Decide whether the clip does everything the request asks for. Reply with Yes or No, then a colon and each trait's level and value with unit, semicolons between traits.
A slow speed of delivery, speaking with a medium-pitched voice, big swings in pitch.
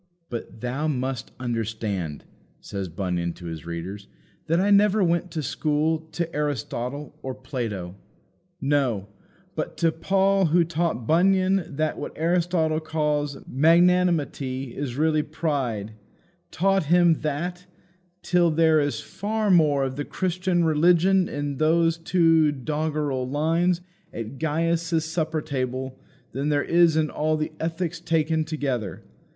No: slow, 130 wpm; medium, 155 Hz; average, 4.2 semitones